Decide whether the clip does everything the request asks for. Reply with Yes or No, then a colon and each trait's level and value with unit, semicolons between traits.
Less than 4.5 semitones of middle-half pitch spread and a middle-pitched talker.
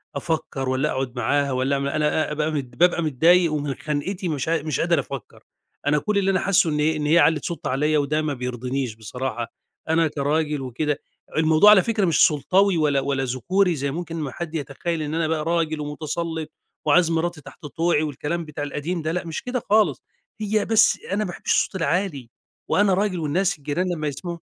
Yes: average, 3.3 semitones; medium, 155 Hz